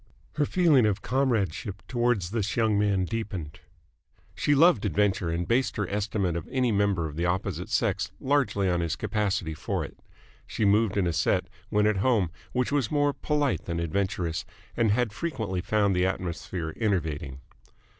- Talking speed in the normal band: Yes, average, 165 wpm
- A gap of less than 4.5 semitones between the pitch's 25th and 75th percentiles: No, average, 4.8 semitones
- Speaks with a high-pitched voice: No, low, 100 Hz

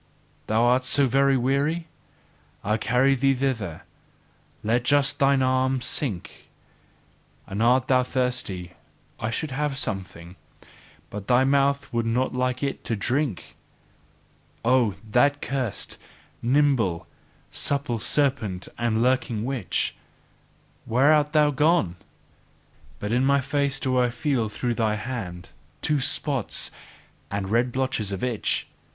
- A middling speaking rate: No, slow, 125 wpm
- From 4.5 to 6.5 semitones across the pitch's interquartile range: No, average, 3.7 semitones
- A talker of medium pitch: No, low, 125 Hz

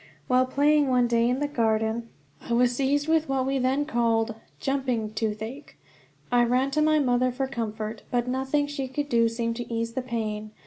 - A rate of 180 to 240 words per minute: Yes, average, 190 wpm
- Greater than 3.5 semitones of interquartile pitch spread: No, average, 2.8 semitones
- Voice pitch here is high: Yes, very high, 250 Hz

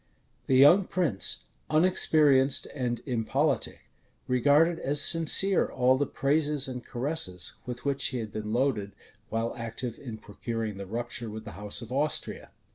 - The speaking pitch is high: No, low, 130 Hz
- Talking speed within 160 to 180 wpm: No, average, 145 wpm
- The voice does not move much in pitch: No, average, 4.4 semitones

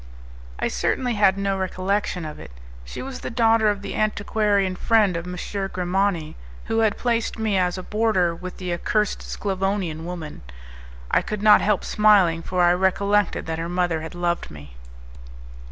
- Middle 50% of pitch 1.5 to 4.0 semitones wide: Yes, average, 3.1 semitones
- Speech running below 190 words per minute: Yes, average, 170 wpm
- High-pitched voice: Yes, high, 195 Hz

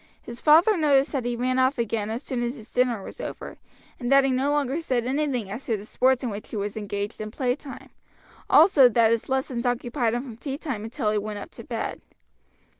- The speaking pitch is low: No, high, 245 Hz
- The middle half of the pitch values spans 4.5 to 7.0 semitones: No, average, 3.4 semitones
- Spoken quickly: Yes, fast, 225 wpm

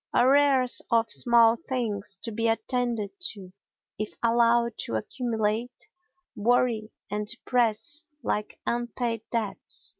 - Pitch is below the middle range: No, high, 230 Hz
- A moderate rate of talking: No, slow, 110 wpm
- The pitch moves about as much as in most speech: No, narrow, 2.2 semitones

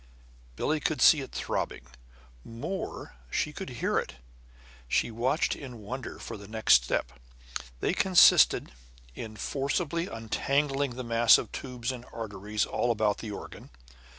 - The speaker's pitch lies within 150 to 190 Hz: No, low, 120 Hz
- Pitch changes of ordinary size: Yes, average, 4.2 semitones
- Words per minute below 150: Yes, average, 140 wpm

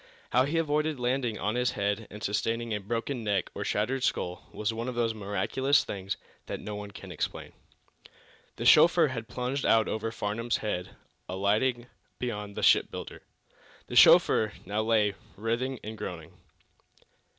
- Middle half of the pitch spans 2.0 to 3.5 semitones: Yes, average, 3.2 semitones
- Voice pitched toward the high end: No, low, 110 Hz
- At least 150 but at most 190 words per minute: Yes, average, 155 wpm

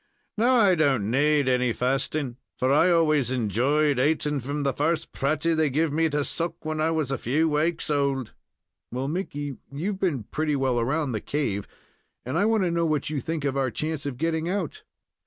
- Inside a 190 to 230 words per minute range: Yes, average, 195 wpm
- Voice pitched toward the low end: No, medium, 150 Hz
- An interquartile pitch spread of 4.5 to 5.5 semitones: No, average, 3.3 semitones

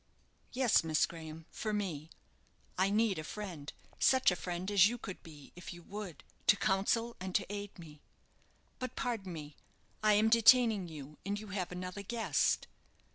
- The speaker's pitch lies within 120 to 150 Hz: No, high, 195 Hz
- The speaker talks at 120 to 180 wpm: Yes, average, 170 wpm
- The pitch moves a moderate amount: Yes, average, 4.0 semitones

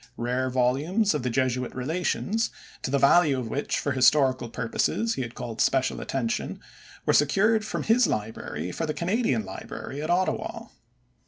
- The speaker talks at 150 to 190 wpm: Yes, average, 160 wpm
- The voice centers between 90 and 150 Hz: Yes, low, 135 Hz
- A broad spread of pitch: Yes, wide, 6.4 semitones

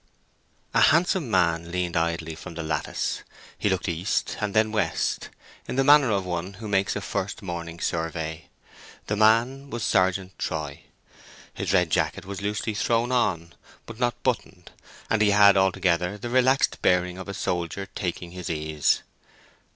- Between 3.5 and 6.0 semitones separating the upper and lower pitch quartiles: Yes, average, 4.3 semitones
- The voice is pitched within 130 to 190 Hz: No, very low, 95 Hz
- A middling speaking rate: Yes, average, 160 wpm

